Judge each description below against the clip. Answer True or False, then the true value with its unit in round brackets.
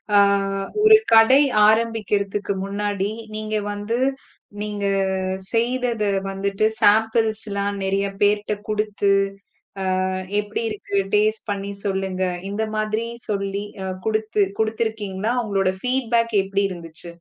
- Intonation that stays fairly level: True (1.8 semitones)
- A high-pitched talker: True (210 Hz)